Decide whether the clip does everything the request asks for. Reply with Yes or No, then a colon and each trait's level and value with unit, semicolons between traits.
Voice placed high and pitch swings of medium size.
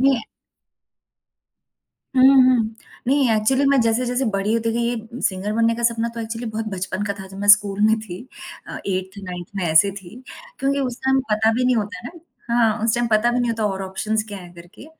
Yes: high, 220 Hz; average, 3.2 semitones